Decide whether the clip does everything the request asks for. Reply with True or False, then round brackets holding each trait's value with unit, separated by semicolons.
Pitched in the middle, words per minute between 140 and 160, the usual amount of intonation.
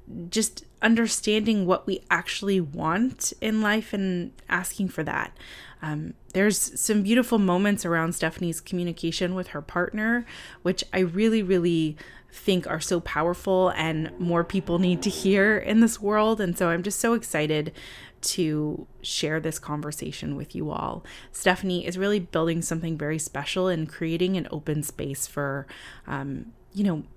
True (180 Hz; 150 wpm; 4.1 semitones)